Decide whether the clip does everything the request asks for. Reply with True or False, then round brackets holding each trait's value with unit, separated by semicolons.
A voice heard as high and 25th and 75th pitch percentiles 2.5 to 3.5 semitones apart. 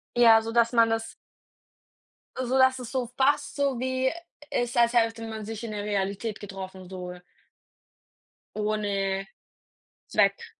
True (225 Hz; 3.1 semitones)